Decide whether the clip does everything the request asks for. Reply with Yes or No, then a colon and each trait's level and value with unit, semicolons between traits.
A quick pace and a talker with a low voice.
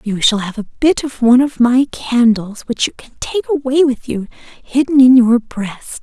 No: fast, 210 wpm; very high, 250 Hz